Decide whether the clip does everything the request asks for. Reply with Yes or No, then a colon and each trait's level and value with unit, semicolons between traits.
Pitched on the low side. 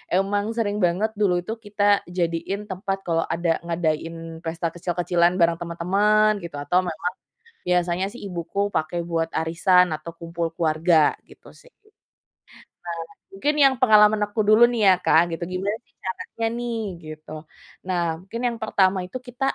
No: medium, 180 Hz